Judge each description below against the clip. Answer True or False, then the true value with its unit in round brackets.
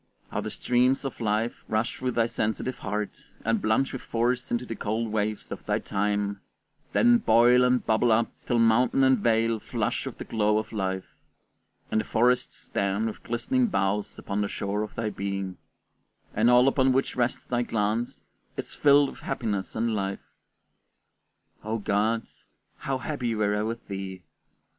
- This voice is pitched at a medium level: False (115 Hz)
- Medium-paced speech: True (170 wpm)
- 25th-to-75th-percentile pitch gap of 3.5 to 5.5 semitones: False (2.9 semitones)